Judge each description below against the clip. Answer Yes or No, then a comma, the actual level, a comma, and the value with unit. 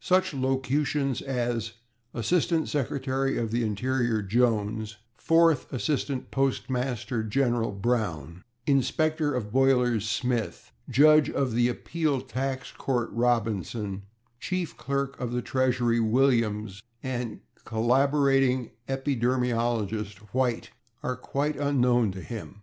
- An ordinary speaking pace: No, slow, 105 wpm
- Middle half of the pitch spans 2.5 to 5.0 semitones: Yes, average, 3.1 semitones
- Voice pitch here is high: No, low, 125 Hz